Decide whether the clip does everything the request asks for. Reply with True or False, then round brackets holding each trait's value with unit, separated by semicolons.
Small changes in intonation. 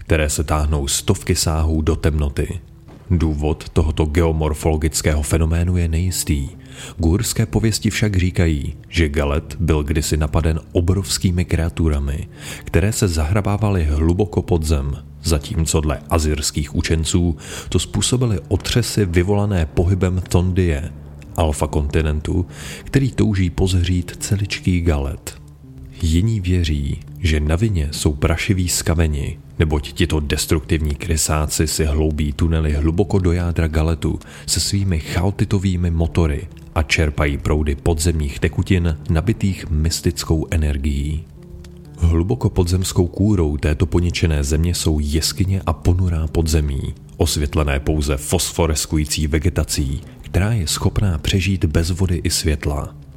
False (3.3 semitones)